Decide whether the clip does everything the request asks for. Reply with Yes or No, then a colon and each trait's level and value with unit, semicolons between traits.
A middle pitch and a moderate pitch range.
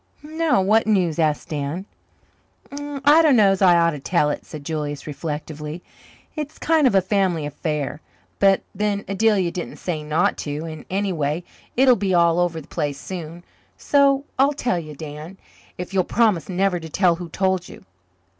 Yes: medium, 180 Hz; average, 4.9 semitones